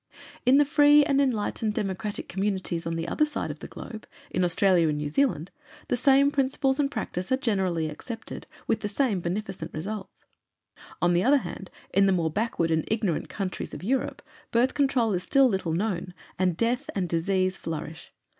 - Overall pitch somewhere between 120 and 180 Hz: No, high, 200 Hz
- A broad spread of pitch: Yes, wide, 6.5 semitones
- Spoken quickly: No, average, 185 wpm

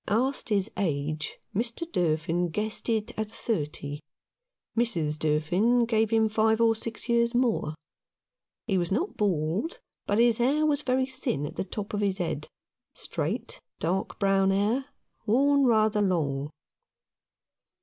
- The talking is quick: No, average, 140 wpm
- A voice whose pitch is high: Yes, high, 215 Hz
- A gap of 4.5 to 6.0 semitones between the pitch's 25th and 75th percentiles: Yes, average, 5.3 semitones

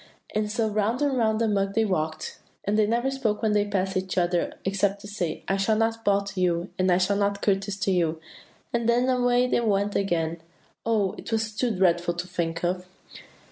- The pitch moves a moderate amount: Yes, average, 3.2 semitones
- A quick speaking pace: Yes, fast, 220 wpm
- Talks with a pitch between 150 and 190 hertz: No, high, 200 Hz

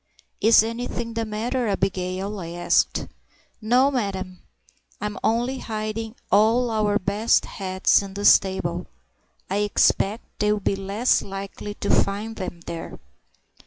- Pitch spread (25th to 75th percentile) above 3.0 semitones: No, narrow, 2.6 semitones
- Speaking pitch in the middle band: No, high, 210 Hz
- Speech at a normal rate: No, slow, 125 wpm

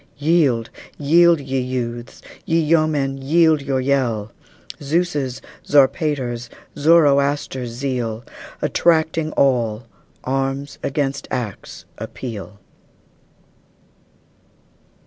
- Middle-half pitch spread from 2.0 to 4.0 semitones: Yes, average, 3.5 semitones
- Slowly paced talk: Yes, slow, 75 wpm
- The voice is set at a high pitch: No, low, 135 Hz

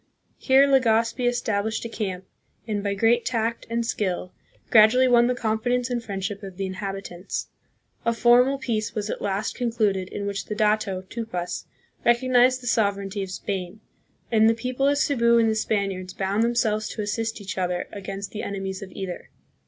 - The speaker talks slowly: No, average, 175 wpm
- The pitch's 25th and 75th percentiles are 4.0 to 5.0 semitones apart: No, average, 3.3 semitones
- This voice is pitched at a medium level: No, high, 215 Hz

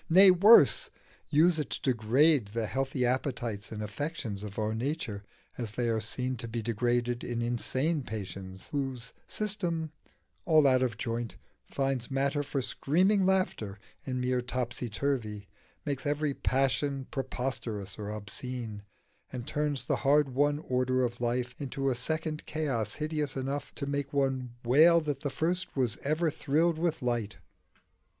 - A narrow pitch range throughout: No, average, 4.0 semitones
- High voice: No, low, 130 Hz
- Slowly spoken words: No, average, 150 wpm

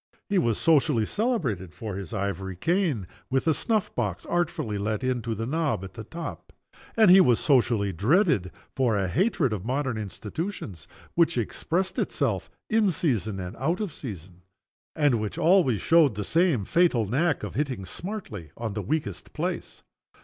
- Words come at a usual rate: Yes, average, 165 wpm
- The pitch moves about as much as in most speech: No, wide, 8.5 semitones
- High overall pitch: No, low, 125 Hz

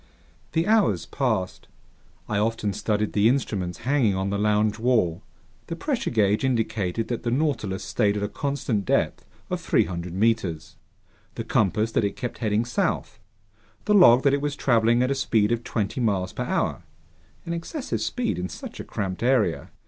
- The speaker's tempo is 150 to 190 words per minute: Yes, average, 170 wpm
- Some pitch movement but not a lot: Yes, average, 4.3 semitones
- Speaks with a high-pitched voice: No, low, 110 Hz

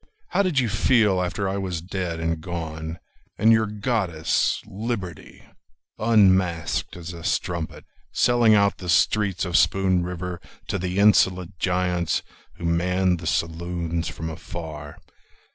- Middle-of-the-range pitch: No, very low, 90 Hz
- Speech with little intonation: No, average, 3.1 semitones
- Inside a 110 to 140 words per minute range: Yes, slow, 135 wpm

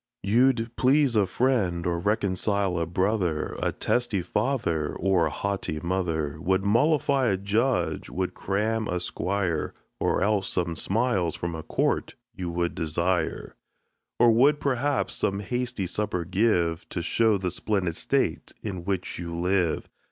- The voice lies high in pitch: No, very low, 95 Hz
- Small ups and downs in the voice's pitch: No, average, 4.5 semitones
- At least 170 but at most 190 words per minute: No, average, 145 wpm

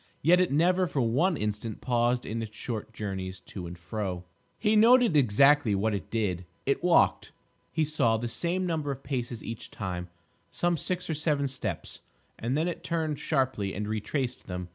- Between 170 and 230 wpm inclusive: Yes, average, 180 wpm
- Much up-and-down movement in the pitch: Yes, wide, 7.0 semitones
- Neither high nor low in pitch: No, low, 120 Hz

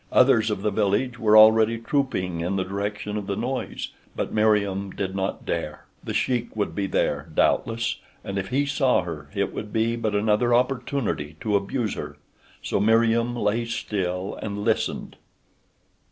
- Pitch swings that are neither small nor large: Yes, average, 3.0 semitones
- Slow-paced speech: No, average, 165 wpm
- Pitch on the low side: Yes, low, 105 Hz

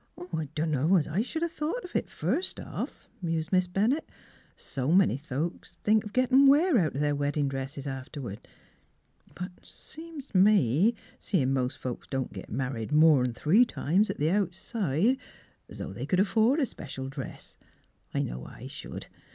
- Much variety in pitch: Yes, wide, 8.0 semitones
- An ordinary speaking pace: Yes, average, 175 wpm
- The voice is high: No, medium, 170 Hz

